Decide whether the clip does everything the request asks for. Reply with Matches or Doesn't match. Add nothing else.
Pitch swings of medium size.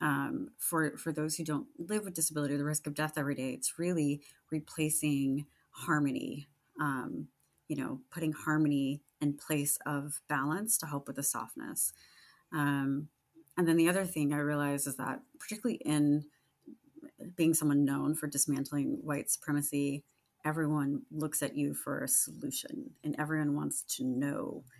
Doesn't match